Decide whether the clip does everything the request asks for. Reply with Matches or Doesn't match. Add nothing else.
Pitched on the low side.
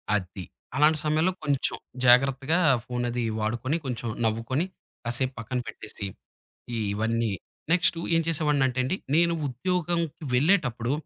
Matches